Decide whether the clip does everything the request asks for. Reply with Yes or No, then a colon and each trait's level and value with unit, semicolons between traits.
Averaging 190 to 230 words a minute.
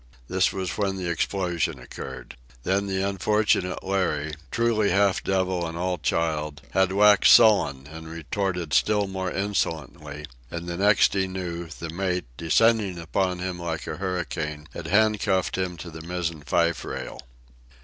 No: average, 150 wpm